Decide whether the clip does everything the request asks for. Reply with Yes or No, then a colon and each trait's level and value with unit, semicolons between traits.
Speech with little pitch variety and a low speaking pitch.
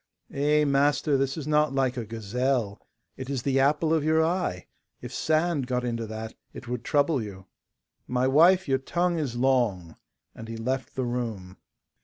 No: average, 4.3 semitones; low, 130 Hz